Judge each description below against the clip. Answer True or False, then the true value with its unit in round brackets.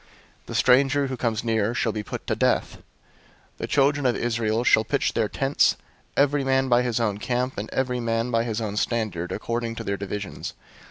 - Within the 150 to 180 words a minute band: False (200 wpm)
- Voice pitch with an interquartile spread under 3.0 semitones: True (2.6 semitones)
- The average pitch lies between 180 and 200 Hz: False (115 Hz)